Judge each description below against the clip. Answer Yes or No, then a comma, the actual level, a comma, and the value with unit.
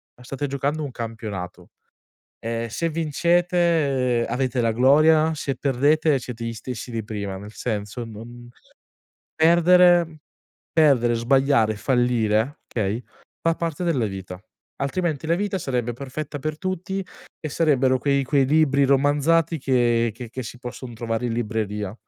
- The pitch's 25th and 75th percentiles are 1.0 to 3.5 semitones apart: No, average, 5.0 semitones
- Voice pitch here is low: Yes, low, 130 Hz